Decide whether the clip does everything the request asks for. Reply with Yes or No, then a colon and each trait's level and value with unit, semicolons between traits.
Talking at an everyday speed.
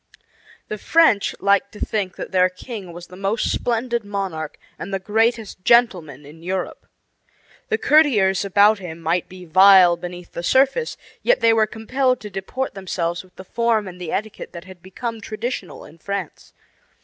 Yes: average, 170 wpm